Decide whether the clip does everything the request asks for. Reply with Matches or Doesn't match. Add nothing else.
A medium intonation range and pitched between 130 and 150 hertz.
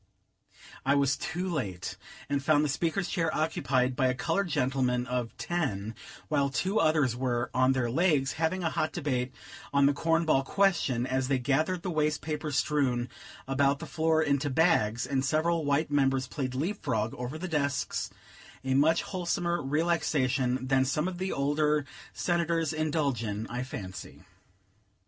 Matches